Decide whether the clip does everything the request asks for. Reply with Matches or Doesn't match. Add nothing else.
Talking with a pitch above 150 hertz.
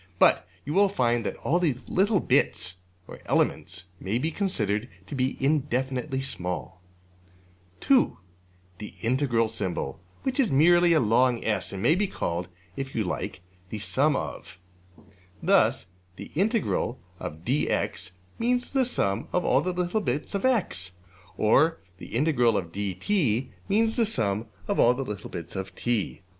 Doesn't match